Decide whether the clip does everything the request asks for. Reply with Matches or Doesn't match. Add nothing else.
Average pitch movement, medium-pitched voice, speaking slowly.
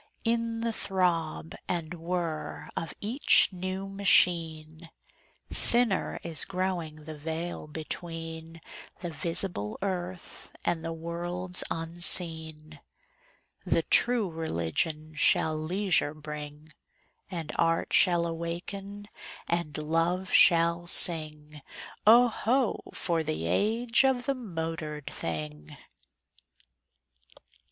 Matches